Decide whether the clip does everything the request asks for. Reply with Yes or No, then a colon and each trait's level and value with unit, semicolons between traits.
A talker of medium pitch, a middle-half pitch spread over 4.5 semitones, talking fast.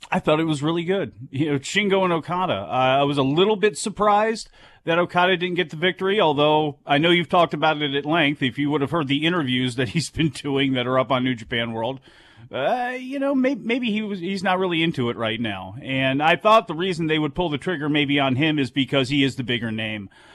Yes: medium, 155 Hz; average, 5.3 semitones; fast, 250 wpm